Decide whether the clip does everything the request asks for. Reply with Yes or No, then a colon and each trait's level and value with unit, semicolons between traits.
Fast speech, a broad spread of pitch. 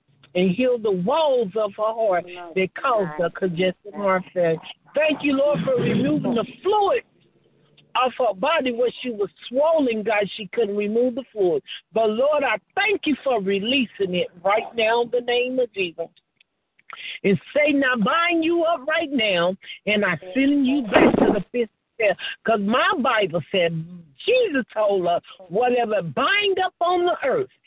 No: average, 170 wpm; wide, 6.8 semitones